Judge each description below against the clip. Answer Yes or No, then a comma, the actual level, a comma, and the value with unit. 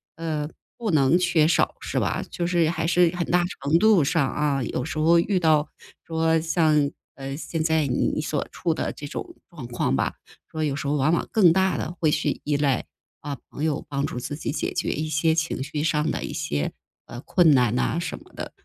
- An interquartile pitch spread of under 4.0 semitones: Yes, average, 2.8 semitones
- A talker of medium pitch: Yes, medium, 155 Hz